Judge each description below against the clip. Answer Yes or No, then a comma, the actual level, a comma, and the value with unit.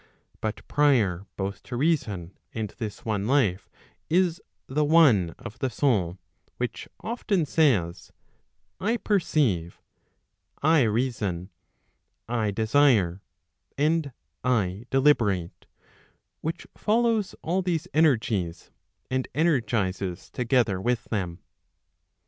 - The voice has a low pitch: Yes, low, 120 Hz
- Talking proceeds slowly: Yes, slow, 100 wpm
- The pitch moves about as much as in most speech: No, wide, 7.4 semitones